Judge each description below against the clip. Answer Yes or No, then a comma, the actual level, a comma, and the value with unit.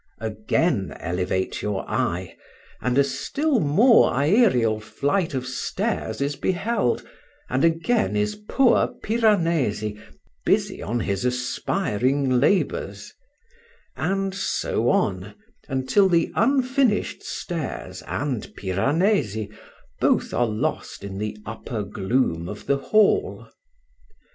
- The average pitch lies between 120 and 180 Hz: Yes, low, 135 Hz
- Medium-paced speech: No, slow, 105 wpm